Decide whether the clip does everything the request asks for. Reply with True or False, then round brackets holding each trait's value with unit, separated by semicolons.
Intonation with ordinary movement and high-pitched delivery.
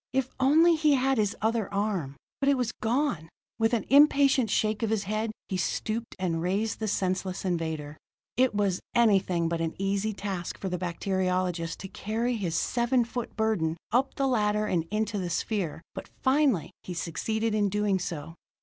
True (4.5 semitones; 210 Hz)